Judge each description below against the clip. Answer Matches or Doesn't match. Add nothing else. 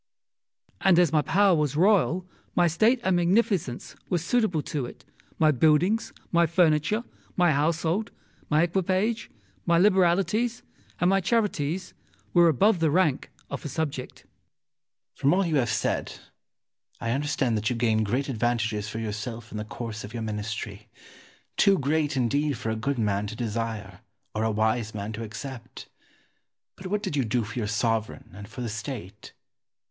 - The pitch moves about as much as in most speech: Doesn't match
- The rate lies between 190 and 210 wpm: Doesn't match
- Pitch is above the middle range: Doesn't match